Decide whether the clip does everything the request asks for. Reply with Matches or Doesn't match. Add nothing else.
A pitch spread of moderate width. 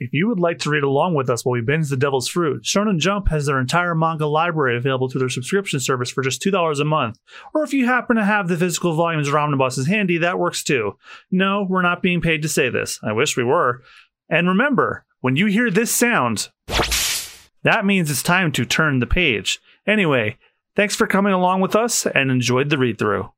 Doesn't match